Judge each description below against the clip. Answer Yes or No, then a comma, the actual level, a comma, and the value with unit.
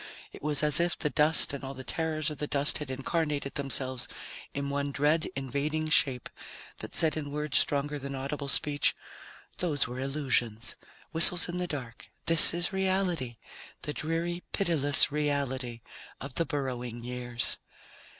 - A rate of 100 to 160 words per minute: Yes, average, 155 wpm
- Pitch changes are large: No, average, 2.9 semitones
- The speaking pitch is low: No, medium, 145 Hz